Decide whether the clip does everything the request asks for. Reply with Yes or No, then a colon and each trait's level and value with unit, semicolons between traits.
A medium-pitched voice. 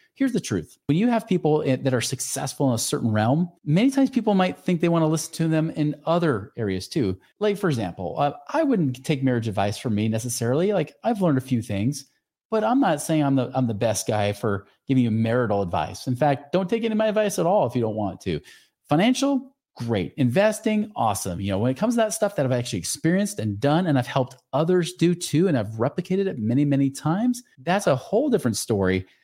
Yes: medium, 145 Hz